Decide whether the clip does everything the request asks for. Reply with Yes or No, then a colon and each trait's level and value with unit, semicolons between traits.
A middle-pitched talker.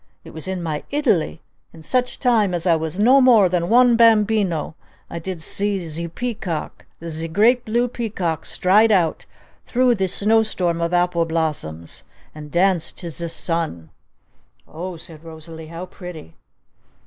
Yes: medium, 175 Hz